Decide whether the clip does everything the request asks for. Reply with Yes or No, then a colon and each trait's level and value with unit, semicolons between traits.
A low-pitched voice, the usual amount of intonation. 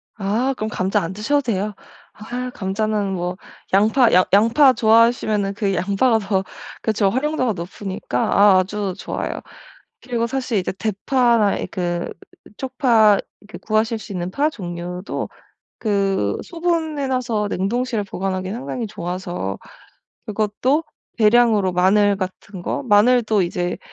No: high, 210 Hz; average, 4.0 semitones